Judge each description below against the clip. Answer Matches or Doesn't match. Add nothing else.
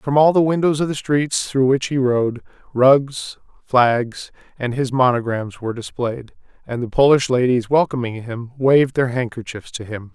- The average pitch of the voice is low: Matches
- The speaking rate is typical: Matches